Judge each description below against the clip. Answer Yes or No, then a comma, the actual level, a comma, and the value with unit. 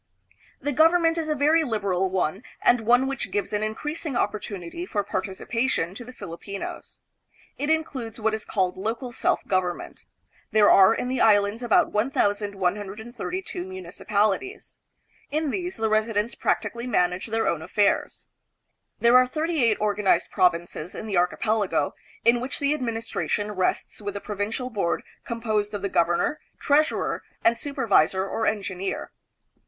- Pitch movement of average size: Yes, average, 4.2 semitones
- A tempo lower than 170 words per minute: Yes, average, 150 wpm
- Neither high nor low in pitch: No, high, 215 Hz